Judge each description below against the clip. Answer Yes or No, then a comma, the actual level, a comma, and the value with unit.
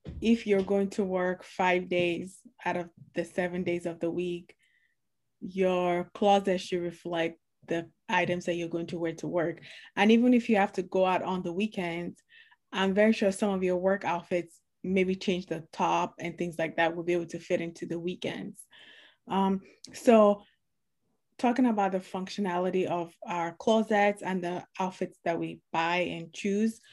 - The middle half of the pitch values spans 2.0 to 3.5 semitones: Yes, narrow, 2.5 semitones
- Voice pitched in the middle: Yes, medium, 180 Hz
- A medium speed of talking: Yes, average, 180 wpm